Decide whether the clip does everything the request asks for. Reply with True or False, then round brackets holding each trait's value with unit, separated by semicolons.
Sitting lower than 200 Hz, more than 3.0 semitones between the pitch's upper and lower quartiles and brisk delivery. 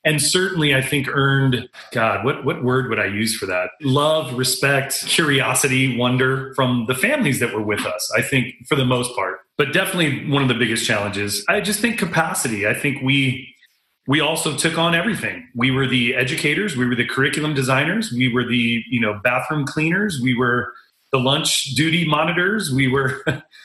False (135 Hz; 3.6 semitones; 190 wpm)